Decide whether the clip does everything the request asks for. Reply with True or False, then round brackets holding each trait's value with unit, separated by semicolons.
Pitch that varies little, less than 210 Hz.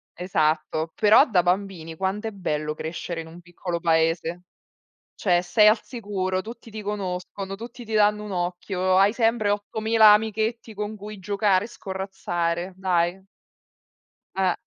False (3.2 semitones; 190 Hz)